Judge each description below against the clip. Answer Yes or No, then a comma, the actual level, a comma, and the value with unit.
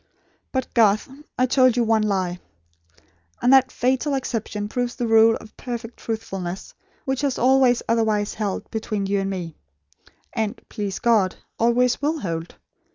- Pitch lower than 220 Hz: No, high, 225 Hz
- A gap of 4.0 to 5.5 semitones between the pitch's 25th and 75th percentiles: No, average, 3.5 semitones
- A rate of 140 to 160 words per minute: Yes, average, 150 wpm